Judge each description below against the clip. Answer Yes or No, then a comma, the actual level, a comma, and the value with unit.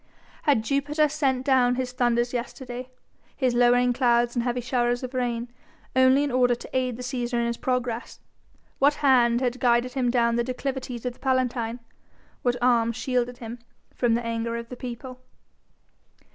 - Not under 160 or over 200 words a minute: Yes, average, 170 wpm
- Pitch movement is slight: Yes, narrow, 1.3 semitones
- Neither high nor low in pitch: No, high, 245 Hz